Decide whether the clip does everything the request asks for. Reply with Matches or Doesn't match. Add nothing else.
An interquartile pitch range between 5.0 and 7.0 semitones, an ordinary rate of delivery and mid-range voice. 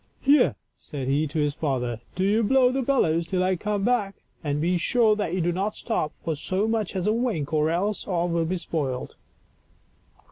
Doesn't match